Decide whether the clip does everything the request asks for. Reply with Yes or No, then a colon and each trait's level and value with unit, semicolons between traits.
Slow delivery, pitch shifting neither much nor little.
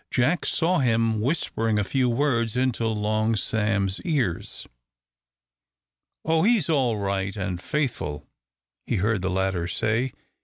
Yes: slow, 125 wpm; average, 4.8 semitones